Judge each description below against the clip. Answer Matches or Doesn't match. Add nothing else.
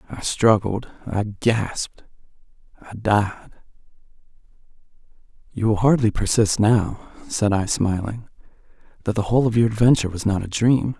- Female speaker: Doesn't match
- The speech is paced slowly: Matches